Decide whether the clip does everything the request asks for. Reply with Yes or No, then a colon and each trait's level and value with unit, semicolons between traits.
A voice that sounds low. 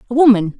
No: high, 235 Hz